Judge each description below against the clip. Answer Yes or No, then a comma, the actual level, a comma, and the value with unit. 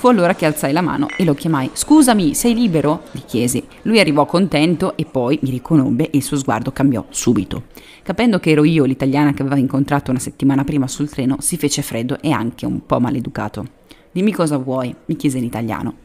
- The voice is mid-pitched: Yes, medium, 145 Hz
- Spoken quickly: Yes, fast, 205 wpm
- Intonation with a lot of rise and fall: No, average, 3.6 semitones